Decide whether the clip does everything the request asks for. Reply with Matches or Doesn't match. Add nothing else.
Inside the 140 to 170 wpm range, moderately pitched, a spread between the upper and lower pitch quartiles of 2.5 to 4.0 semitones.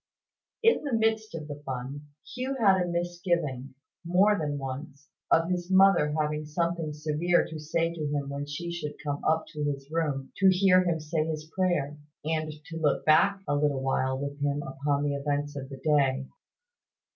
Doesn't match